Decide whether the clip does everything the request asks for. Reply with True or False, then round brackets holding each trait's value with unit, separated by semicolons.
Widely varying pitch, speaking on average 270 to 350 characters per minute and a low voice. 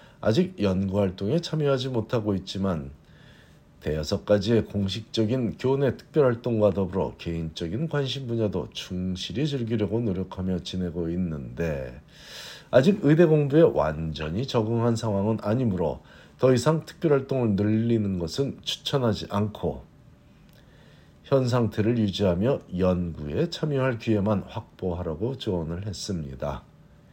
True (5.7 semitones; 290 characters per minute; 105 Hz)